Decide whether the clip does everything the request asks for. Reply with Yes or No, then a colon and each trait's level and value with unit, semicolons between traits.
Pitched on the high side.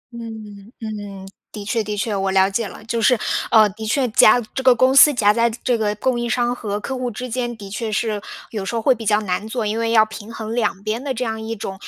Yes: high, 220 Hz